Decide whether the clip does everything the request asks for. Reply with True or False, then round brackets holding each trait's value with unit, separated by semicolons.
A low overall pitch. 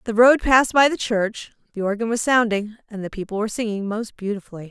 False (220 Hz)